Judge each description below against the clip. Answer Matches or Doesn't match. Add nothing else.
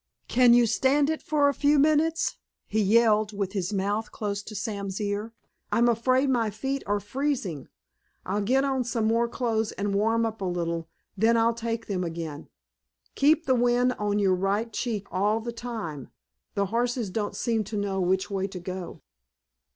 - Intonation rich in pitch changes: Doesn't match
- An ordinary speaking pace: Matches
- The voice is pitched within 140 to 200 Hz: Doesn't match